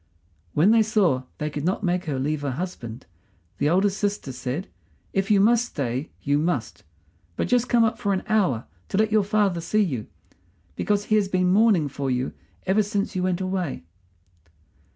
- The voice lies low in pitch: No, medium, 185 Hz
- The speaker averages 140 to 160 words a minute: No, average, 185 wpm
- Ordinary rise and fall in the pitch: No, wide, 6.3 semitones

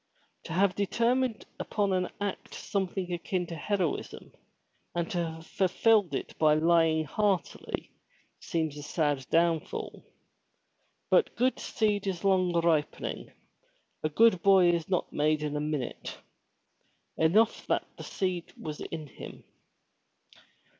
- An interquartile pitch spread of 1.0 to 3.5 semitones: No, average, 3.9 semitones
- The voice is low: No, medium, 175 Hz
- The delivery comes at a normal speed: No, slow, 125 wpm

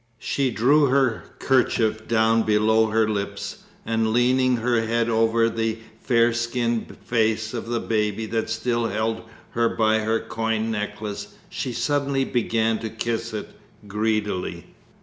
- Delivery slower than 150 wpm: Yes, average, 140 wpm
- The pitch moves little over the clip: Yes, narrow, 1.3 semitones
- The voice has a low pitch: Yes, low, 115 Hz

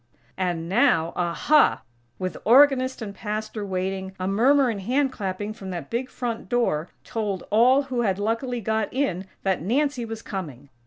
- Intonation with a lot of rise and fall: No, average, 4.6 semitones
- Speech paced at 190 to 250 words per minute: No, average, 160 wpm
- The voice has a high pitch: Yes, high, 215 Hz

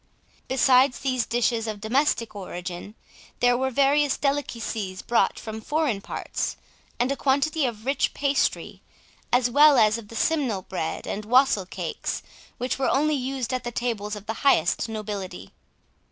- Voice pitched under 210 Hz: No, high, 245 Hz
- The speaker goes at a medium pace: Yes, average, 155 wpm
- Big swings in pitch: No, average, 4.3 semitones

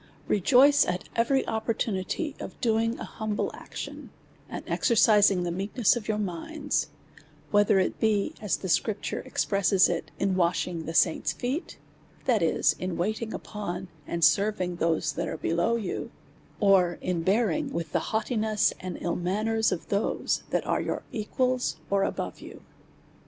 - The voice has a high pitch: Yes, high, 205 Hz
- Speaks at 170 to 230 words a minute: No, average, 155 wpm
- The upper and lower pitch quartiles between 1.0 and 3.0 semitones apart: No, average, 3.9 semitones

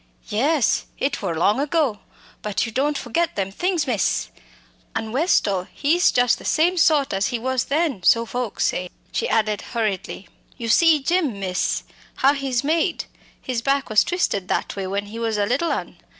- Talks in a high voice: Yes, high, 245 Hz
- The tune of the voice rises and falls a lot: Yes, wide, 6.2 semitones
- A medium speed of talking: Yes, average, 180 wpm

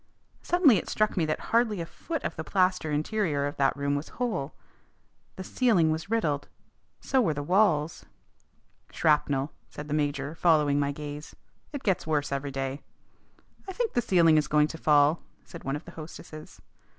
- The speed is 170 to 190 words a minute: Yes, average, 175 wpm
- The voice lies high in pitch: No, medium, 155 Hz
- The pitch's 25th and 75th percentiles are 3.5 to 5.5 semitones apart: Yes, average, 4.5 semitones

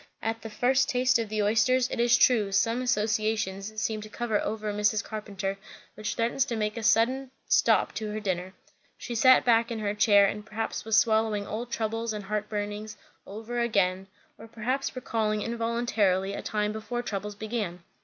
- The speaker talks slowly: No, average, 175 wpm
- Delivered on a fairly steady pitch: Yes, narrow, 1.9 semitones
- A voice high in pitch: Yes, high, 215 Hz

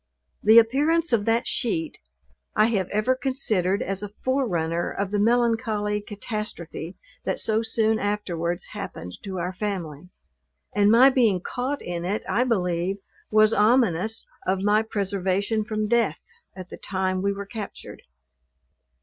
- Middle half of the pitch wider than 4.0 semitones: No, average, 3.3 semitones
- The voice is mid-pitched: No, high, 210 Hz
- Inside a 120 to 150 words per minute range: Yes, average, 140 wpm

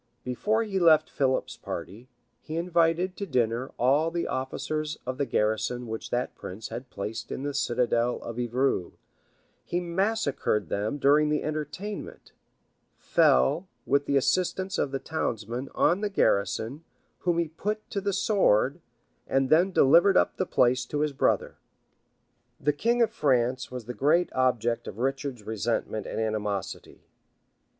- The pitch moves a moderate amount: No, wide, 6.1 semitones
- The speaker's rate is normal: Yes, average, 150 wpm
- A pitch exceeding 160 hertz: No, low, 135 Hz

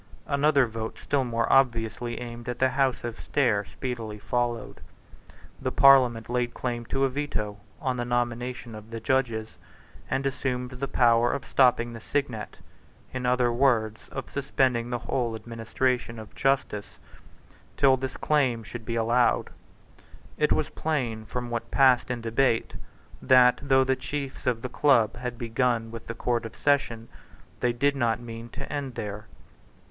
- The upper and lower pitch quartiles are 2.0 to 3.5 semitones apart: Yes, narrow, 2.4 semitones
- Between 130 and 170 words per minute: Yes, average, 160 wpm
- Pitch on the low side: Yes, low, 120 Hz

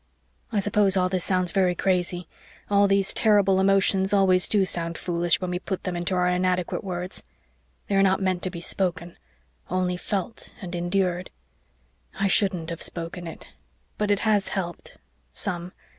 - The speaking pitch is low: No, medium, 185 Hz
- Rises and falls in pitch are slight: Yes, narrow, 1.8 semitones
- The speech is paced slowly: No, average, 160 wpm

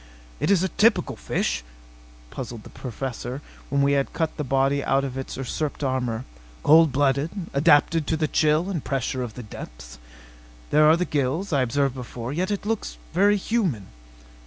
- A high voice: No, medium, 140 Hz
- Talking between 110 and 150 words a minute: No, average, 175 wpm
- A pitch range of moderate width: Yes, average, 4.0 semitones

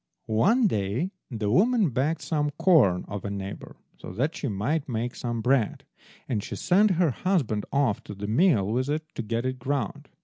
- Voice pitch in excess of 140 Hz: No, low, 130 Hz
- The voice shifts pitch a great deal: Yes, wide, 7.1 semitones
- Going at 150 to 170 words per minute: No, average, 190 wpm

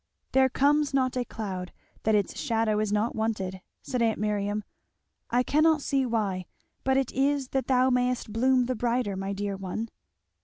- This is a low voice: No, high, 230 Hz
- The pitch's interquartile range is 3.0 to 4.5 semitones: Yes, average, 4.0 semitones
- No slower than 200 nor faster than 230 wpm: No, average, 170 wpm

